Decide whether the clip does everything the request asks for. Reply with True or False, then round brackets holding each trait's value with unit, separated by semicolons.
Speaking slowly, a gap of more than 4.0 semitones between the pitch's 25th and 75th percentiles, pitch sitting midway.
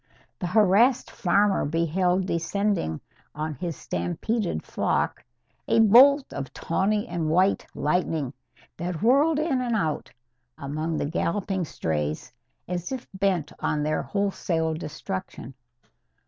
True (120 wpm; 5.0 semitones; 180 Hz)